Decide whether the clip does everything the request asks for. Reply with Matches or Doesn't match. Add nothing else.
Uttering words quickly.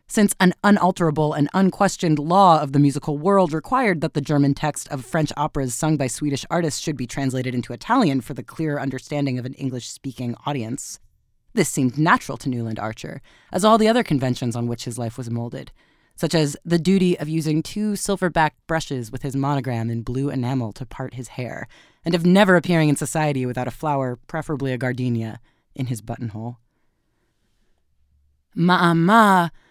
Doesn't match